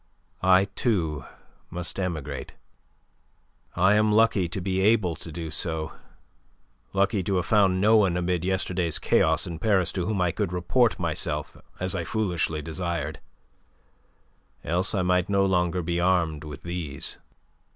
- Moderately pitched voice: No, very low, 90 Hz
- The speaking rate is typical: Yes, average, 145 wpm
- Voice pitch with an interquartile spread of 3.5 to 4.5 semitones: No, average, 2.7 semitones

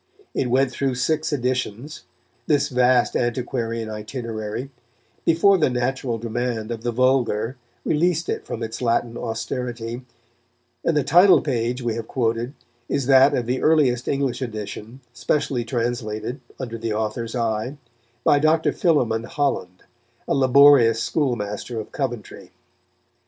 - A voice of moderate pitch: No, low, 125 Hz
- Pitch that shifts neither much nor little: Yes, average, 3.2 semitones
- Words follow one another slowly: Yes, slow, 130 wpm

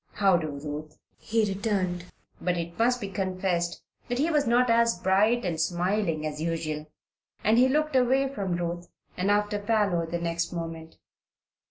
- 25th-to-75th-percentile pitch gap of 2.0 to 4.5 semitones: No, average, 5.1 semitones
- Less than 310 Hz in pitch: Yes, medium, 185 Hz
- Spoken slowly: No, average, 165 wpm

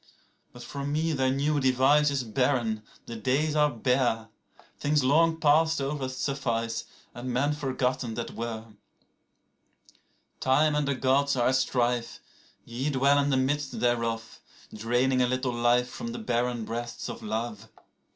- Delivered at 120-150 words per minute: Yes, average, 140 wpm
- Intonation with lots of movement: No, average, 3.1 semitones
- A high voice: No, low, 130 Hz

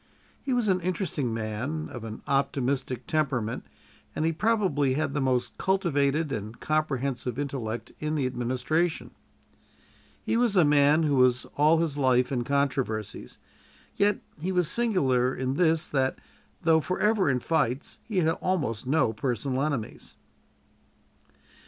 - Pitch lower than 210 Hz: Yes, medium, 140 Hz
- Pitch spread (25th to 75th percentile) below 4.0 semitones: No, average, 4.3 semitones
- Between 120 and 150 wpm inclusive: Yes, average, 140 wpm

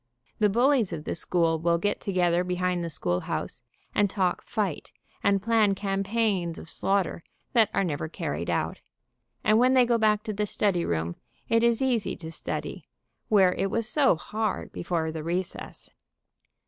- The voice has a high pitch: Yes, high, 195 Hz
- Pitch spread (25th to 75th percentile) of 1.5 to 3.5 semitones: No, average, 4.2 semitones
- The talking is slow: No, average, 170 wpm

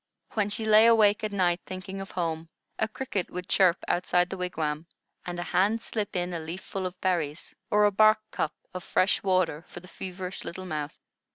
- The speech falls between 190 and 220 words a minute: Yes, average, 200 wpm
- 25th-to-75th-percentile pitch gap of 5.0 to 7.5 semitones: No, narrow, 2.6 semitones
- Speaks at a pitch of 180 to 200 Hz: Yes, medium, 185 Hz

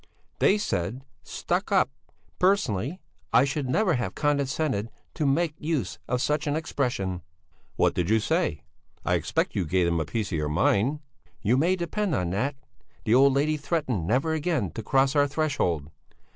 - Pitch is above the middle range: No, low, 135 Hz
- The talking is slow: No, average, 170 wpm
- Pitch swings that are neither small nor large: No, wide, 7.5 semitones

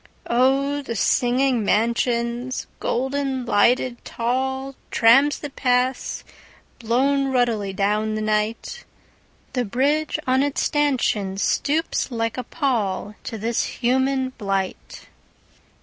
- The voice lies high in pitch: Yes, very high, 250 Hz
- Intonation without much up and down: No, average, 3.1 semitones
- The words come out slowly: Yes, slow, 85 wpm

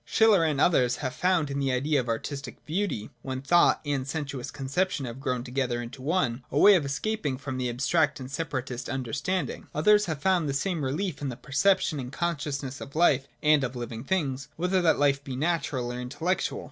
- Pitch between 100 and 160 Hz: Yes, medium, 140 Hz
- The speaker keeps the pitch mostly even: No, average, 4.4 semitones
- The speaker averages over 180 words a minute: Yes, average, 200 wpm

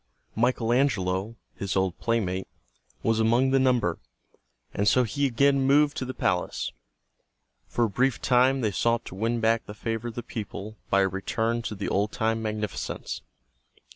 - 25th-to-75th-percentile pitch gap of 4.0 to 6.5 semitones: No, average, 3.4 semitones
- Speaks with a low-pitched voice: Yes, low, 115 Hz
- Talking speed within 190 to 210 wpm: No, average, 170 wpm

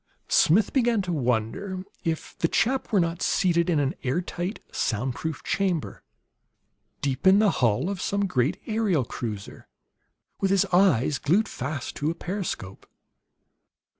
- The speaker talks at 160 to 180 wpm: No, average, 145 wpm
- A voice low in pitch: No, medium, 170 Hz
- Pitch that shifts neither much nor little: No, wide, 6.6 semitones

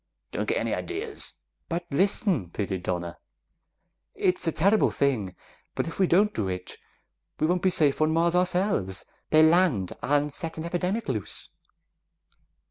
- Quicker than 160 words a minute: No, average, 150 wpm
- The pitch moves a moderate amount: No, wide, 8.9 semitones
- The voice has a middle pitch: Yes, medium, 165 Hz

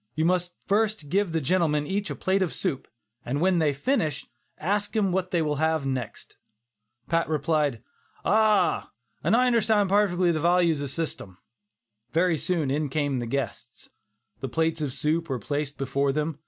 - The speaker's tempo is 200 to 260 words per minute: No, average, 175 wpm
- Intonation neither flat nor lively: Yes, average, 4.5 semitones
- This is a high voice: No, medium, 160 Hz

